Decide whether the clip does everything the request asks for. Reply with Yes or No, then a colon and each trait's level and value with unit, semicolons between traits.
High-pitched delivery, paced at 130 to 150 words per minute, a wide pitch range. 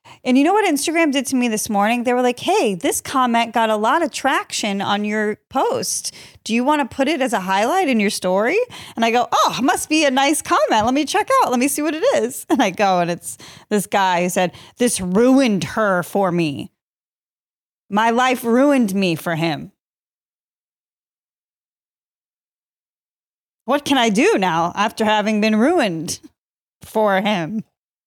No: high, 230 Hz; average, 185 wpm; wide, 5.7 semitones